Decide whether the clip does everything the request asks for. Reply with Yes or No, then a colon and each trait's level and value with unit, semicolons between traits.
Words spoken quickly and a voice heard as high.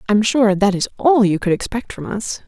Yes: fast, 240 wpm; high, 210 Hz